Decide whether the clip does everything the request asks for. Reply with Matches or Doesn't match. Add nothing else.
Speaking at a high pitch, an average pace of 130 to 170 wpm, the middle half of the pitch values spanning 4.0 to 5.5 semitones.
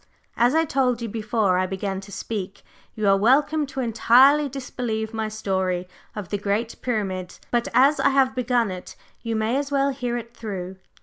Doesn't match